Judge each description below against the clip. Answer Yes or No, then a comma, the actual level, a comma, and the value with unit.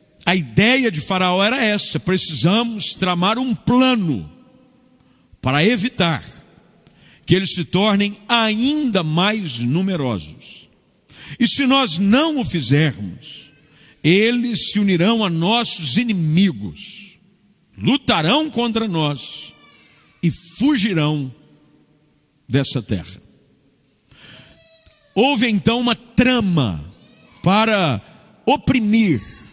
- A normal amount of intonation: No, wide, 6.8 semitones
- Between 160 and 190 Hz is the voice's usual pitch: Yes, medium, 185 Hz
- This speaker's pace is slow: Yes, slow, 90 wpm